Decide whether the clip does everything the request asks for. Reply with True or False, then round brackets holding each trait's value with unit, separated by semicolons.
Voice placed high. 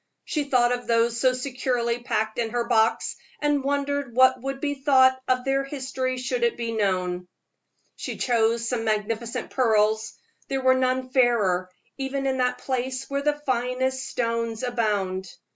True (250 Hz)